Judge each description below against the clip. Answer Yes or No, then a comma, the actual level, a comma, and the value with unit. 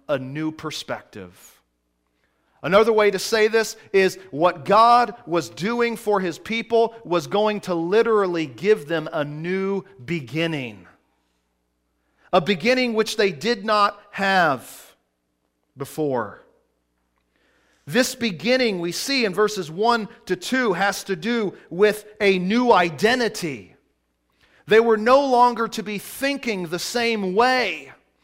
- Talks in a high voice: Yes, high, 195 Hz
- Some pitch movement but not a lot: No, wide, 6.4 semitones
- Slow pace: Yes, slow, 125 wpm